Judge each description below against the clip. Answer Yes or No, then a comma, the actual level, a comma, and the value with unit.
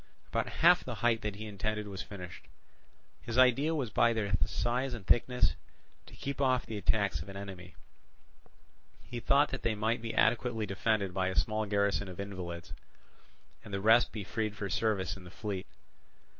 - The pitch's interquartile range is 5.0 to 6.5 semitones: No, average, 3.2 semitones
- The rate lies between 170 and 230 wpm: Yes, average, 180 wpm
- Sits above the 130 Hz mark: No, low, 105 Hz